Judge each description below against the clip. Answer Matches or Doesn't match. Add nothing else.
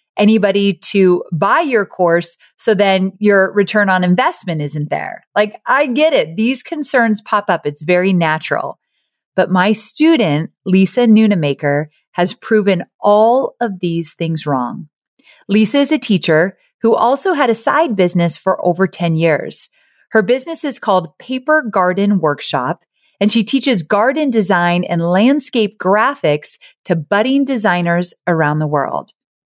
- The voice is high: Matches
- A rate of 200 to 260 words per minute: Doesn't match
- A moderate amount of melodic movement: Matches